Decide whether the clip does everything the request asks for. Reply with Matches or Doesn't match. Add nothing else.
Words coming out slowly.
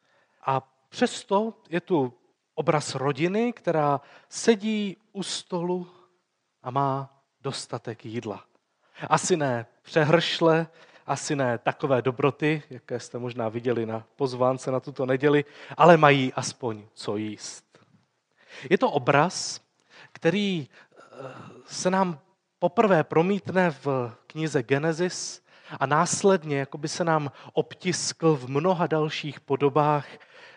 Matches